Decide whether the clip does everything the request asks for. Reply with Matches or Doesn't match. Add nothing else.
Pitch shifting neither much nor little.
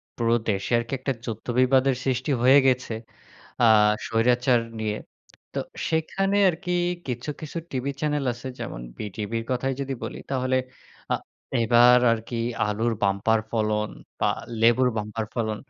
Matches